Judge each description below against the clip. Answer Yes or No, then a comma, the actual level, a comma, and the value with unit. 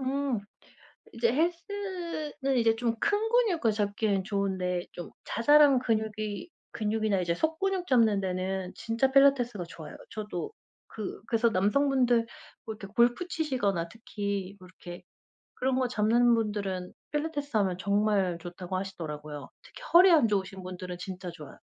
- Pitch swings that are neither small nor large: No, wide, 5.9 semitones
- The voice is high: Yes, high, 215 Hz